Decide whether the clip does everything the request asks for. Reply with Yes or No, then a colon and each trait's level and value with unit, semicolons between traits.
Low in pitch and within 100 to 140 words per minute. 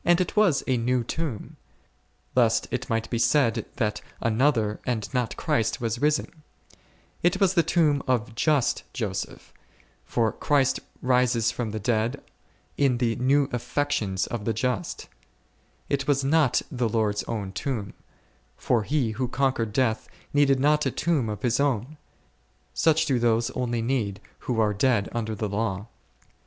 No: low, 125 Hz; average, 150 wpm